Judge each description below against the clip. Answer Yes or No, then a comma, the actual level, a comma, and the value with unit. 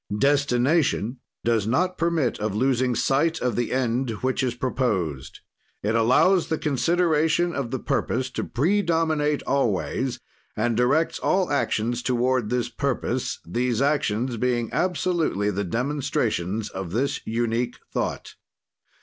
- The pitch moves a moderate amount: Yes, average, 4.3 semitones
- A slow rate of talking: Yes, slow, 125 wpm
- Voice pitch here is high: No, low, 125 Hz